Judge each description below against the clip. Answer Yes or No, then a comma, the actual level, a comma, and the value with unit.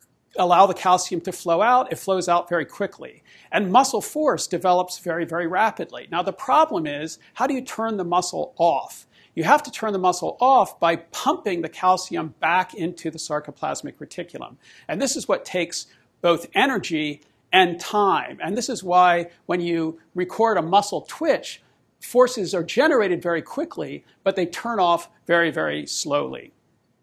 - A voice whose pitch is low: No, medium, 180 Hz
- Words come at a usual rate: Yes, average, 170 wpm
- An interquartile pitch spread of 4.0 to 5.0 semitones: Yes, average, 4.4 semitones